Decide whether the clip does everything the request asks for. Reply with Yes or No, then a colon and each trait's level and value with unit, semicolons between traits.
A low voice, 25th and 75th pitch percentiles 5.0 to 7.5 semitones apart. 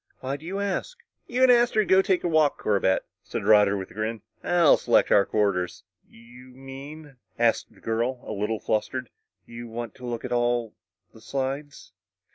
Yes: low, 125 Hz; wide, 5.4 semitones